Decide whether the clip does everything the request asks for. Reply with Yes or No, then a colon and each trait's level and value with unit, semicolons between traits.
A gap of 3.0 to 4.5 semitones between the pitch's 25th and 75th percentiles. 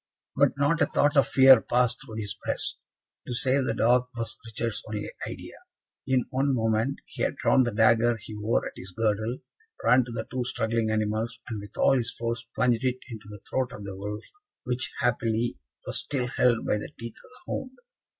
No: narrow, 2.5 semitones